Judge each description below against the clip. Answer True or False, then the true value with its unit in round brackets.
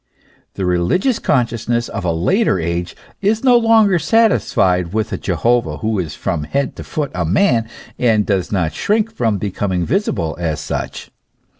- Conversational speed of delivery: True (160 wpm)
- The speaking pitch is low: True (110 Hz)